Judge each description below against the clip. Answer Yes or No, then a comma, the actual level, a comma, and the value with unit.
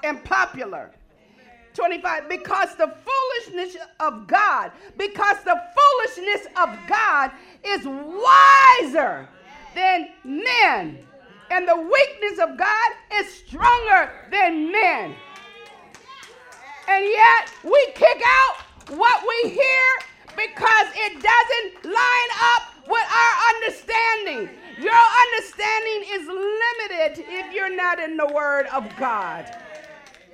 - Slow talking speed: Yes, slow, 105 wpm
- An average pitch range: No, wide, 5.9 semitones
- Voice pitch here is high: Yes, very high, 375 Hz